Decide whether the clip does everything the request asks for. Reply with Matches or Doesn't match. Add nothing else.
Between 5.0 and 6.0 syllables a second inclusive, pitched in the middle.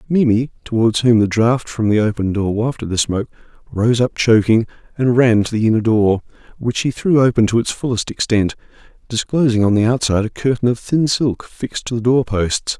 Doesn't match